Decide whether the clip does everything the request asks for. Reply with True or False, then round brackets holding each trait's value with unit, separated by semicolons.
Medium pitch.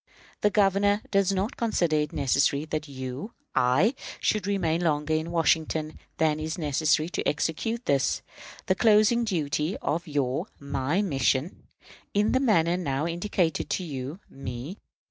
True (160 Hz)